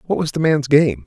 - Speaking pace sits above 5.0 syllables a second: Yes, 5.5 syllables/s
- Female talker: No, male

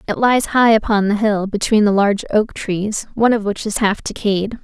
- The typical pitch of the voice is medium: No, high, 210 Hz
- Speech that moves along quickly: Yes, fast, 220 wpm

